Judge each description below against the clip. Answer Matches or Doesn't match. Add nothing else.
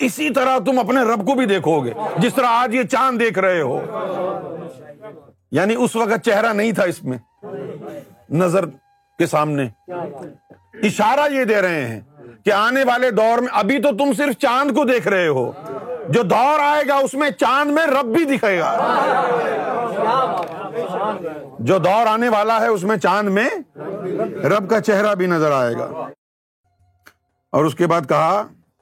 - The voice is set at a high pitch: Matches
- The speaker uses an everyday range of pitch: Doesn't match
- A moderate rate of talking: Matches